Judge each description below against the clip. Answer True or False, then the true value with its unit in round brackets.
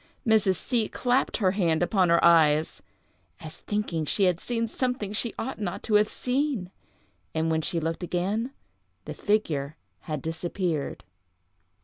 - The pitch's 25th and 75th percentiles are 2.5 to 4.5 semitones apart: False (5.1 semitones)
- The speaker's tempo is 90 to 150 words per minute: True (145 wpm)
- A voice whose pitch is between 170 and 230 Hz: True (185 Hz)